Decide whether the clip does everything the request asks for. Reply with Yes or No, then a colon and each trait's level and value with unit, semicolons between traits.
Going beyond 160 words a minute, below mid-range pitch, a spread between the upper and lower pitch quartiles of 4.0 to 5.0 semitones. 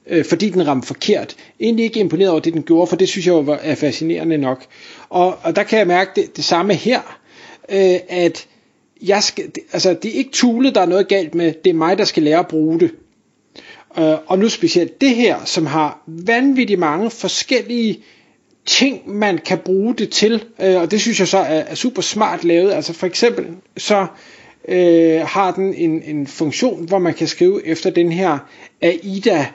No: average, 205 wpm; medium, 185 Hz; average, 4.3 semitones